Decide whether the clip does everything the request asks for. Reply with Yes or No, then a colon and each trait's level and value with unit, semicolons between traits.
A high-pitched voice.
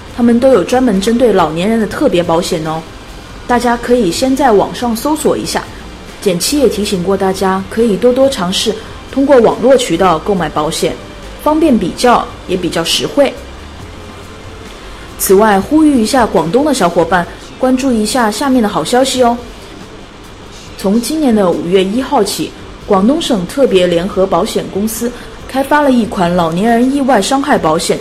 Yes: high, 215 Hz